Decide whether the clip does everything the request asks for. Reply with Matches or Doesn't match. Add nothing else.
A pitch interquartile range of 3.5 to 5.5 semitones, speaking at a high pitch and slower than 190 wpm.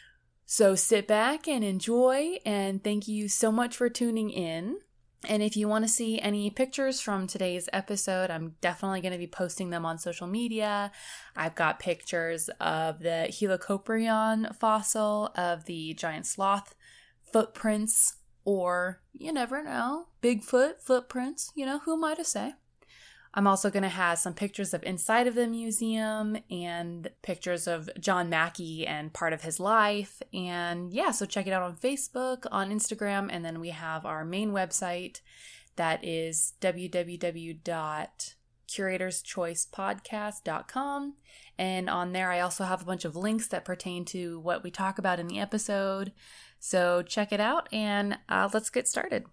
Matches